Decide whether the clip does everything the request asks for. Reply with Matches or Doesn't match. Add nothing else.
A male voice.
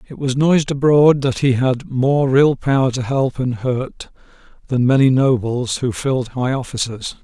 Matches